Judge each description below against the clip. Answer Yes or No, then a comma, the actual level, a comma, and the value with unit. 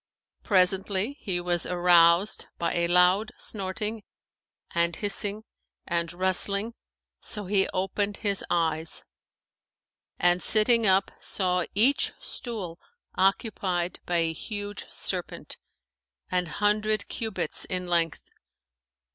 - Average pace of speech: No, slow, 105 wpm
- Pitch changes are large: No, average, 3.0 semitones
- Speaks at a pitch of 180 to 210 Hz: Yes, high, 190 Hz